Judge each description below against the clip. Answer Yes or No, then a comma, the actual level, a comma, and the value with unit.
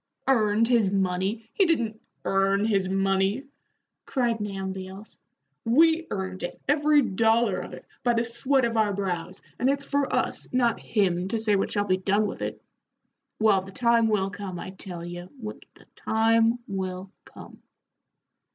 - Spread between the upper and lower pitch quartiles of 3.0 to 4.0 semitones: Yes, average, 3.4 semitones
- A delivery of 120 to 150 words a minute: No, average, 160 wpm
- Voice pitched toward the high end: Yes, high, 210 Hz